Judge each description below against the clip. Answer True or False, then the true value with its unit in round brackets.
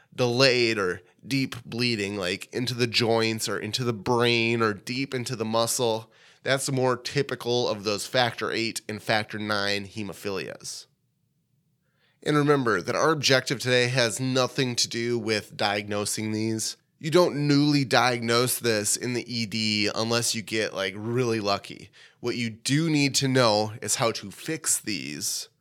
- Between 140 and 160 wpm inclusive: True (155 wpm)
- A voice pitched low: True (120 Hz)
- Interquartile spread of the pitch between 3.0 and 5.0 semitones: True (3.3 semitones)